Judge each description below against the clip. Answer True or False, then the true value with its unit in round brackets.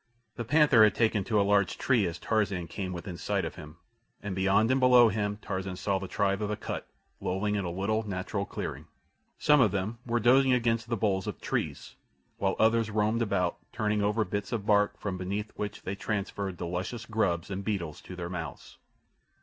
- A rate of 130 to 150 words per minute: False (200 wpm)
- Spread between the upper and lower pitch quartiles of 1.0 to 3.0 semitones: True (2.7 semitones)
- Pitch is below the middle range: True (105 Hz)